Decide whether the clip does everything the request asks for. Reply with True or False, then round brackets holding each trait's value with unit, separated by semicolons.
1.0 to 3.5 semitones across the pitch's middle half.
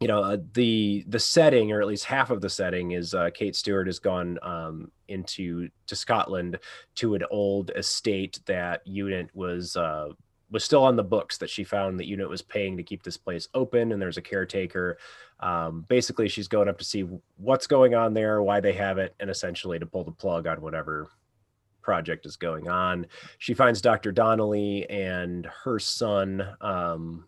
True (2.8 semitones)